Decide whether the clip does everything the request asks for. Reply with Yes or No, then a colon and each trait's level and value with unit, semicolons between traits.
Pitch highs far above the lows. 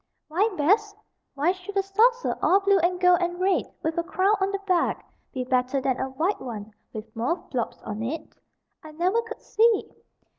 Yes: wide, 6.9 semitones